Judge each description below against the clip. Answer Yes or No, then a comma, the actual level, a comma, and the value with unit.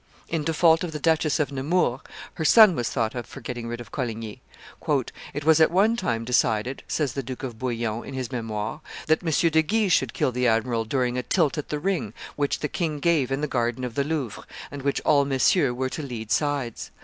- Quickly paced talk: Yes, fast, 225 wpm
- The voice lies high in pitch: No, low, 135 Hz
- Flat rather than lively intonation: No, average, 4.6 semitones